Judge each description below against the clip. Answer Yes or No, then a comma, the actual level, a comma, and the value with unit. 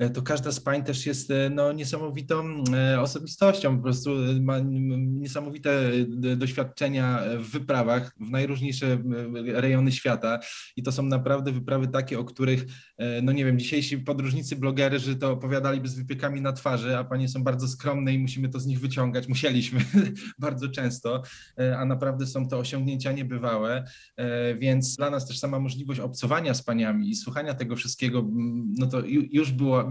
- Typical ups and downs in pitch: No, narrow, 1.6 semitones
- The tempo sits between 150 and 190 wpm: Yes, average, 155 wpm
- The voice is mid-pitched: No, low, 130 Hz